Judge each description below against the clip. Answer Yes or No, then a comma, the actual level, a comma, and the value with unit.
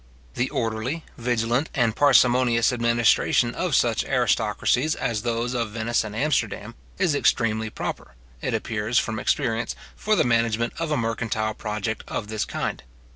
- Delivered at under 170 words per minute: Yes, average, 145 wpm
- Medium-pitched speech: No, low, 115 Hz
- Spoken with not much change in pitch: Yes, narrow, 2.1 semitones